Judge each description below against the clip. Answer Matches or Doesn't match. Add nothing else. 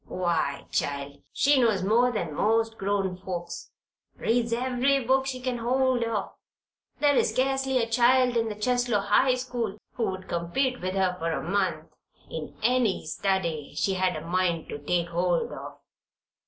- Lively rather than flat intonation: Matches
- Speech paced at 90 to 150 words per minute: Doesn't match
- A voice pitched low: Doesn't match